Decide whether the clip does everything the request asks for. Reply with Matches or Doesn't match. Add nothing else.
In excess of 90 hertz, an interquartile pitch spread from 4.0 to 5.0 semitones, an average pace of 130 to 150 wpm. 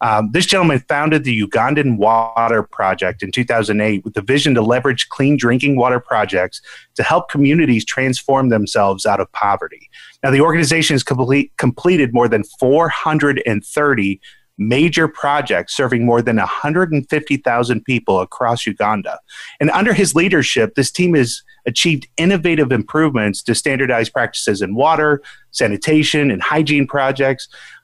Matches